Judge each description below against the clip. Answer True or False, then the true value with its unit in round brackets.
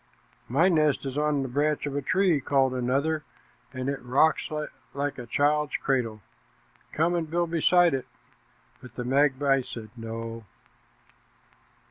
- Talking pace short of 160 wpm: True (140 wpm)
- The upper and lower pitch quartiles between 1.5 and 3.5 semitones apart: True (3.2 semitones)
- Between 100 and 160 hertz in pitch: True (140 Hz)